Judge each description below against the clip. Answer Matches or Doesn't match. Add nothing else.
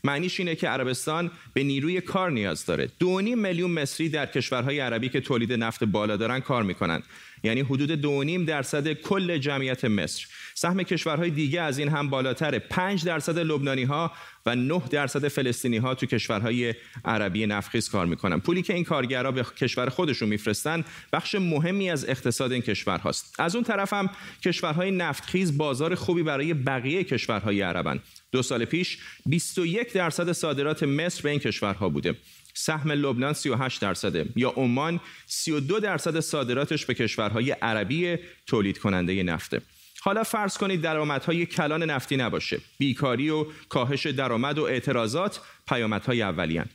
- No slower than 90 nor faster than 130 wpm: Doesn't match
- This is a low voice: Doesn't match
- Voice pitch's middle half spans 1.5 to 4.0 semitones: Doesn't match